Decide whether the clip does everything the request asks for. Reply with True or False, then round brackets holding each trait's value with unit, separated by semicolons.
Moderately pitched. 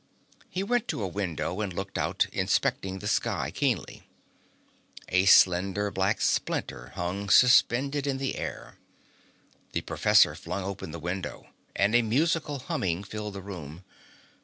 False (100 Hz)